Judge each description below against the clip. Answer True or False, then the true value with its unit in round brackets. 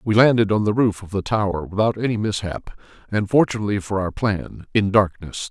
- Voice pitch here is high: False (105 Hz)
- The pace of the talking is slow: False (195 wpm)